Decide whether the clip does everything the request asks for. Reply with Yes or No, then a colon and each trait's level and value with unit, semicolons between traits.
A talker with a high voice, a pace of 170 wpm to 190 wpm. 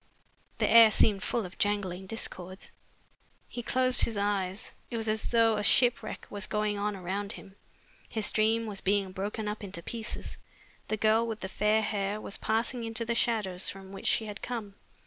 Yes: high, 210 Hz; average, 185 wpm